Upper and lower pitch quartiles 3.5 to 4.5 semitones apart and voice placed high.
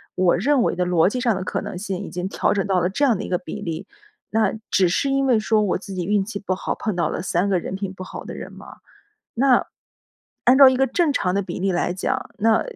Yes: average, 4.1 semitones; high, 195 Hz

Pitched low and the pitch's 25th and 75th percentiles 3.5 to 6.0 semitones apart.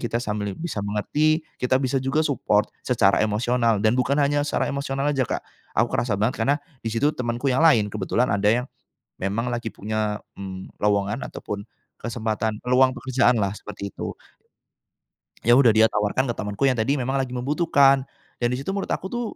Yes: low, 120 Hz; average, 4.3 semitones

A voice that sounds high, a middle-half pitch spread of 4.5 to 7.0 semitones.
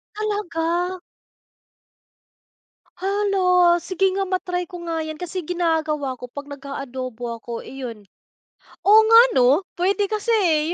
Yes: very high, 345 Hz; average, 5.3 semitones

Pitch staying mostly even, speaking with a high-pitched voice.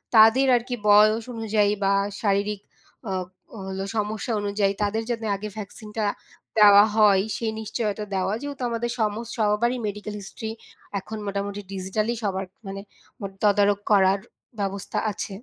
Yes: narrow, 1.8 semitones; high, 210 Hz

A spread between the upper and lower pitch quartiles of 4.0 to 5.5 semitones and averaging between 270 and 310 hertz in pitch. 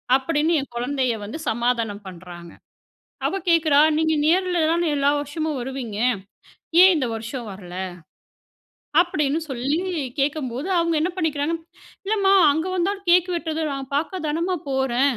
Yes: average, 5.1 semitones; very high, 290 Hz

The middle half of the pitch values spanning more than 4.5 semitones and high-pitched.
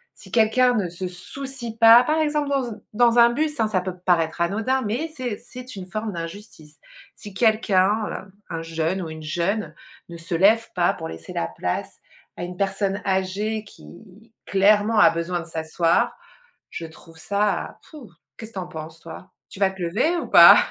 Yes: average, 4.9 semitones; high, 195 Hz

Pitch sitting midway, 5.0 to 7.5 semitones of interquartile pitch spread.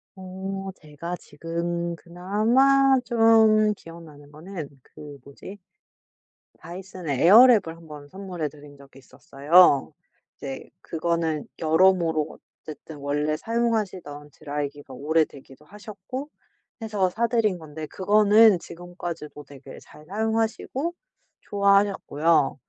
Yes: medium, 170 Hz; wide, 5.4 semitones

